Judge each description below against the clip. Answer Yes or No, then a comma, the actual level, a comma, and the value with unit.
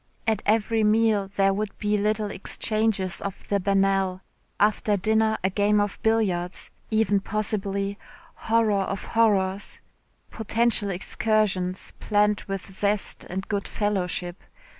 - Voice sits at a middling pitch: No, high, 205 Hz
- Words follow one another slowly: Yes, slow, 120 wpm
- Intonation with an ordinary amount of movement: No, narrow, 1.8 semitones